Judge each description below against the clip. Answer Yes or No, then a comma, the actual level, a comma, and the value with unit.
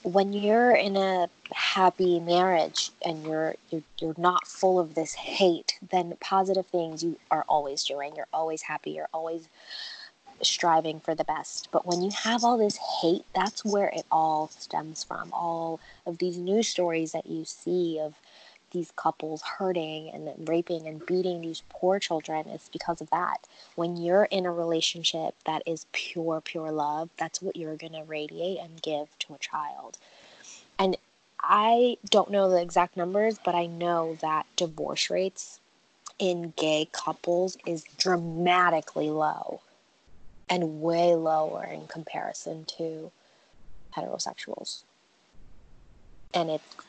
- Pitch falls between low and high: Yes, medium, 170 Hz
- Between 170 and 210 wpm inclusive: No, average, 150 wpm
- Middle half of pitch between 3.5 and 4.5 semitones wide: No, narrow, 2.5 semitones